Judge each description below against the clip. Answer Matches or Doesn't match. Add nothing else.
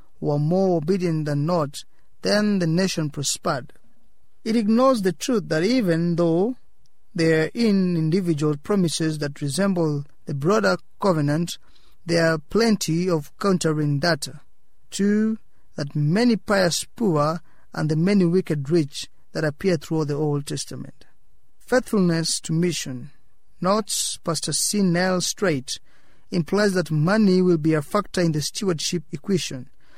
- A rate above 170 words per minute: Doesn't match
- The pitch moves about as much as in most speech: Matches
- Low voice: Doesn't match